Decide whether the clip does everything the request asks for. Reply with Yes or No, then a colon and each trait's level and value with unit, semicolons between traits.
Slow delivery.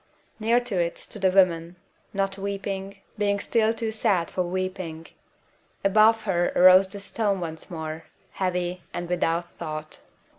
No: average, 145 wpm